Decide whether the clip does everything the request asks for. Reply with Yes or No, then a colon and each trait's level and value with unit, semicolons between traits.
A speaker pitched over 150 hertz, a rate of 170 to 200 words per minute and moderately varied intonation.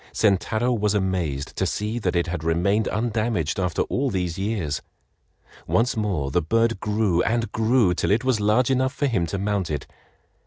No: low, 105 Hz; average, 180 wpm; average, 4.3 semitones